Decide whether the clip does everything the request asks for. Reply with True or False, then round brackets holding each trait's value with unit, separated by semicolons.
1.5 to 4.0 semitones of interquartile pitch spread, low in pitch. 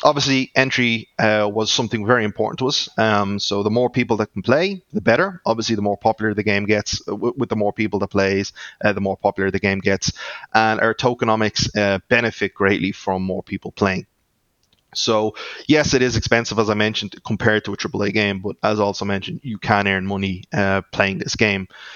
True (2.7 semitones; 110 Hz)